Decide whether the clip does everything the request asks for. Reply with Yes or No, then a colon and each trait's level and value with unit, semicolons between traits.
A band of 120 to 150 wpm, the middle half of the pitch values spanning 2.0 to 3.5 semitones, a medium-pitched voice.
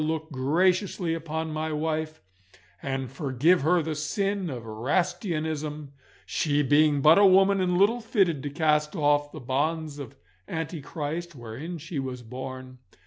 Yes: average, 140 wpm; average, 3.2 semitones; medium, 155 Hz